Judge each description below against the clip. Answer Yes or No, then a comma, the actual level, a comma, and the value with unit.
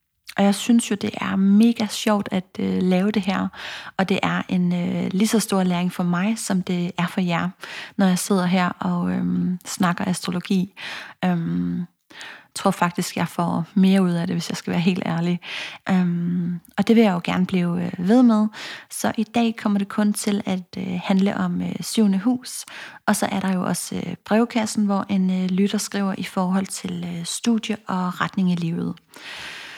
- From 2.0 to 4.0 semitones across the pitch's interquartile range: Yes, average, 2.7 semitones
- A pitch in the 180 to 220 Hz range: Yes, high, 190 Hz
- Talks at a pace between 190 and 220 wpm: Yes, average, 200 wpm